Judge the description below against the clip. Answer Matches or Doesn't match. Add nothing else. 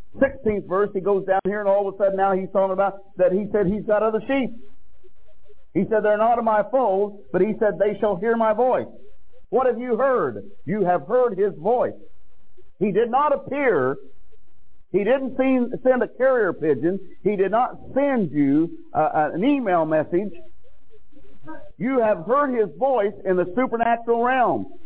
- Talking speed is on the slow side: Doesn't match